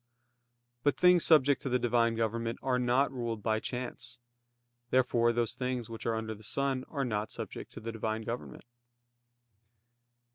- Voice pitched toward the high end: No, low, 120 Hz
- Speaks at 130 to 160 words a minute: Yes, average, 155 wpm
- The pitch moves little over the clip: Yes, narrow, 2.3 semitones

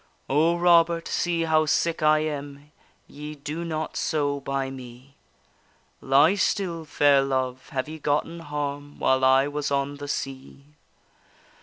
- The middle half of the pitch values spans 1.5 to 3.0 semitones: Yes, narrow, 2.5 semitones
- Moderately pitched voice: Yes, medium, 145 Hz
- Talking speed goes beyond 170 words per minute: No, average, 140 wpm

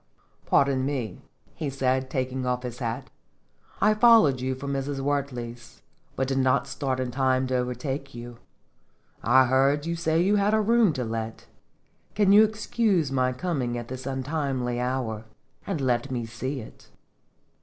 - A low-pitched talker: Yes, low, 130 Hz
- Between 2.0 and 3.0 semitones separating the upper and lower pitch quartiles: Yes, narrow, 2.5 semitones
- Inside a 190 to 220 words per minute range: No, average, 165 wpm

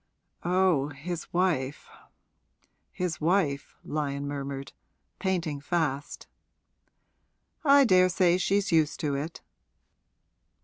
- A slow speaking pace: Yes, slow, 85 wpm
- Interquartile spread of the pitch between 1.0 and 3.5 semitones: No, average, 4.4 semitones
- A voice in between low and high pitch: Yes, medium, 160 Hz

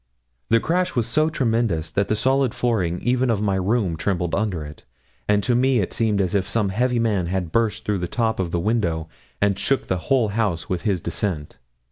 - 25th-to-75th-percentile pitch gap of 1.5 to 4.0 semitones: No, average, 4.5 semitones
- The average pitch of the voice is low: Yes, low, 105 Hz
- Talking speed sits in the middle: No, fast, 210 wpm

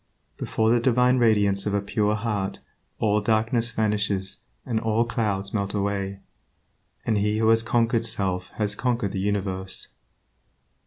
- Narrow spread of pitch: Yes, narrow, 2.3 semitones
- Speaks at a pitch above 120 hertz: No, low, 105 Hz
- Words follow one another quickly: No, average, 145 wpm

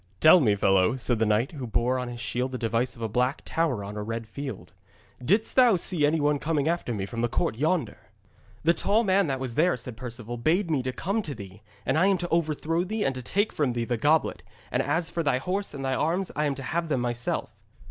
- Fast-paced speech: Yes, fast, 250 wpm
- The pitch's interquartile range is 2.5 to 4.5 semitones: No, wide, 5.6 semitones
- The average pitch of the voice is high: No, low, 135 Hz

